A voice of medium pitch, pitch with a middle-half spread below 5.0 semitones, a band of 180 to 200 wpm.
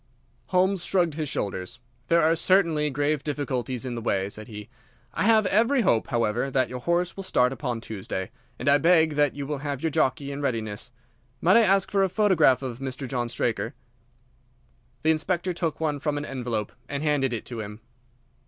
No: medium, 145 Hz; wide, 5.4 semitones; average, 190 wpm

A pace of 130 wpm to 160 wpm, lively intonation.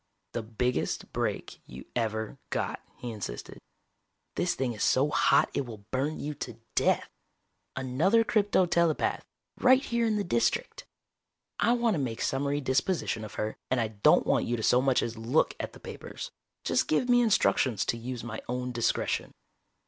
No: average, 170 wpm; wide, 6.8 semitones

